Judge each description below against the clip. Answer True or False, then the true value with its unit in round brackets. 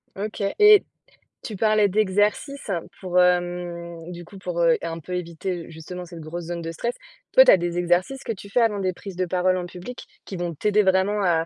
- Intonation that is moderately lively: True (3.1 semitones)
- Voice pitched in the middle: True (180 Hz)